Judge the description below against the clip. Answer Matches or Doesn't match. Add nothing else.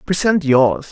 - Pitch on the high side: Doesn't match